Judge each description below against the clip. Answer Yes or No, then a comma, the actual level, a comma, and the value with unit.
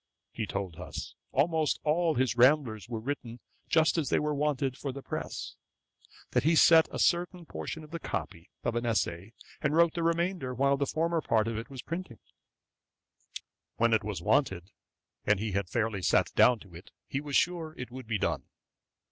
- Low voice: Yes, low, 130 Hz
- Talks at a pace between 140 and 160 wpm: No, average, 190 wpm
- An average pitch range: No, wide, 6.1 semitones